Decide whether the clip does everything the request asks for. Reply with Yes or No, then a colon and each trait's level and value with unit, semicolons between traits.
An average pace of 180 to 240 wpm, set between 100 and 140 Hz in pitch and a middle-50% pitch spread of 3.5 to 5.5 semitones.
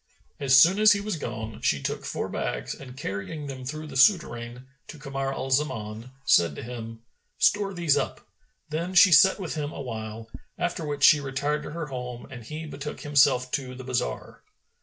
Yes: average, 185 wpm; low, 135 Hz; average, 4.0 semitones